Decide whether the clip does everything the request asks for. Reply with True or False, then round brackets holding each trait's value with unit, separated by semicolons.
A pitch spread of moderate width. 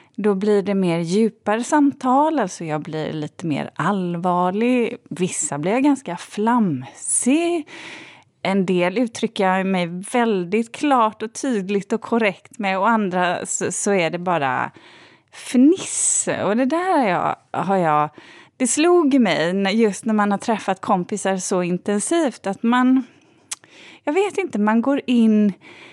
False (5.7 semitones)